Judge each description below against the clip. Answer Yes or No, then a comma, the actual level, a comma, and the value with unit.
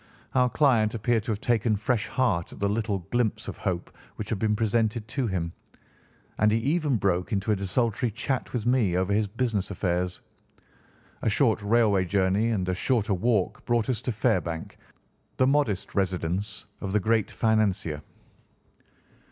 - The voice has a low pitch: Yes, low, 105 Hz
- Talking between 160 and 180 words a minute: Yes, average, 165 wpm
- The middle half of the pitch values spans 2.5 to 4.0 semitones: Yes, average, 3.5 semitones